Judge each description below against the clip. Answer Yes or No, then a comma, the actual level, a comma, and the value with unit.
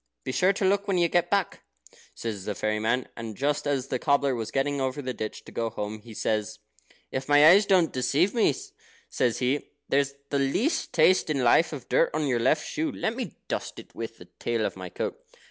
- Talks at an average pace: No, fast, 220 wpm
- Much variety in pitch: Yes, wide, 6.4 semitones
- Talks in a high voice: No, medium, 140 Hz